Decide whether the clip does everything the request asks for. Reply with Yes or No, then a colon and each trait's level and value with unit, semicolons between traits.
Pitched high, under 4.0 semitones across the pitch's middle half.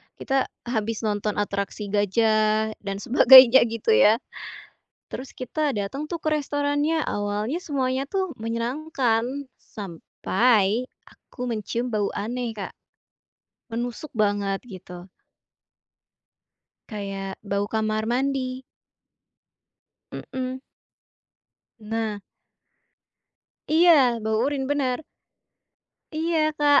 No: high, 230 Hz; average, 4.4 semitones